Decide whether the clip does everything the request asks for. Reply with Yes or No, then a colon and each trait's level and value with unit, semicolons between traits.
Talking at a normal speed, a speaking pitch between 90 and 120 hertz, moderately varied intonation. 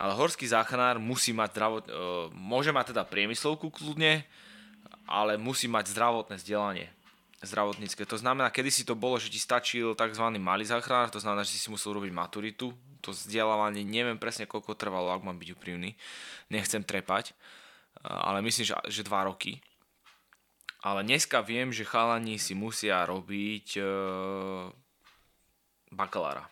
Yes: average, 140 wpm; low, 110 Hz; average, 3.2 semitones